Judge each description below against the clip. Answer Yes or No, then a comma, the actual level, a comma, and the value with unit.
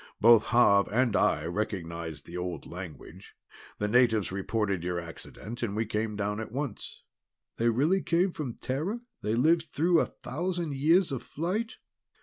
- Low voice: Yes, low, 115 Hz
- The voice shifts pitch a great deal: Yes, wide, 7.4 semitones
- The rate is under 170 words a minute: Yes, average, 155 wpm